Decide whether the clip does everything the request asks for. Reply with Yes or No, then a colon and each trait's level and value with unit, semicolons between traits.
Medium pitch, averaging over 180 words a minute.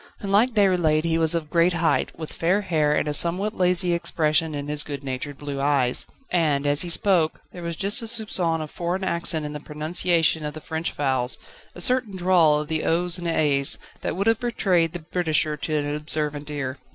Yes: medium, 160 Hz; average, 200 wpm